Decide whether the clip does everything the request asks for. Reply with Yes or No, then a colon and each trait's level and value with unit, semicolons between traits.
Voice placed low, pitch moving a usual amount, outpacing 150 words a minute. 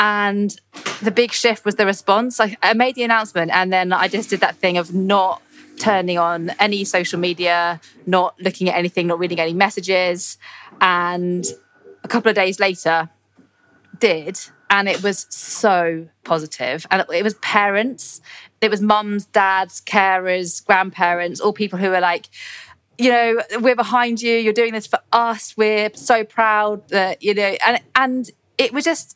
No: high, 195 Hz; average, 3.7 semitones; average, 170 wpm